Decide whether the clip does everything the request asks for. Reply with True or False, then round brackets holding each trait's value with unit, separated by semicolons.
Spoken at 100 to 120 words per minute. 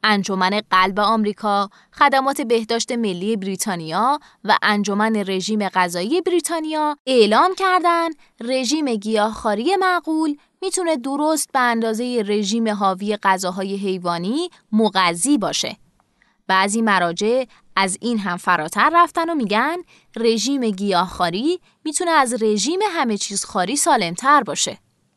True (110 wpm)